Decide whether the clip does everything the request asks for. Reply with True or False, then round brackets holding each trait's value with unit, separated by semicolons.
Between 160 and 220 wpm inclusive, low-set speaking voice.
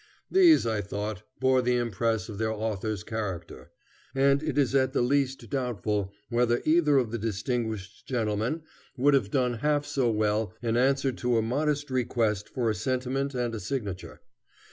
True (165 wpm; 120 Hz)